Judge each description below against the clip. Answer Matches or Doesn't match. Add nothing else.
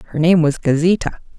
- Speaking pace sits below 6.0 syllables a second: Doesn't match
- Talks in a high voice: Doesn't match